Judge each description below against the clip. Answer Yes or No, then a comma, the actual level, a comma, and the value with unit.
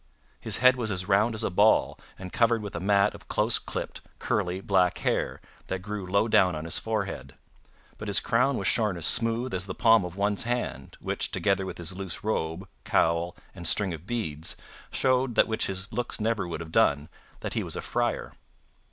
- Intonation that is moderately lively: Yes, average, 3.8 semitones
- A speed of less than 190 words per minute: No, fast, 205 wpm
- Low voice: Yes, low, 100 Hz